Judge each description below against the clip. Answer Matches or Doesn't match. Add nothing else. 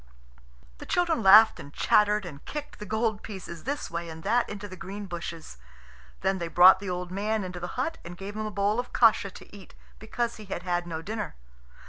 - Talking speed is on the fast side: Matches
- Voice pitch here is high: Matches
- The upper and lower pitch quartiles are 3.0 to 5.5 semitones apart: Matches